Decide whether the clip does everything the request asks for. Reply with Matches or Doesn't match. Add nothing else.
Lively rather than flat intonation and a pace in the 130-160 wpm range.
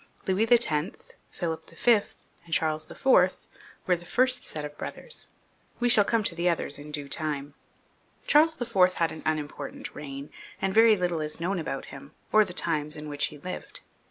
Doesn't match